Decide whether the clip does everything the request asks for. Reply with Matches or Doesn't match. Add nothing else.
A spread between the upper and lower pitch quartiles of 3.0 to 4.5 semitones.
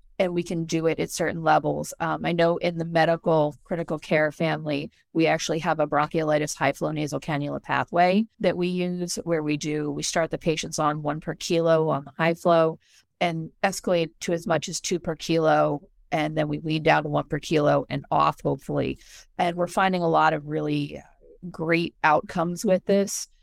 Doesn't match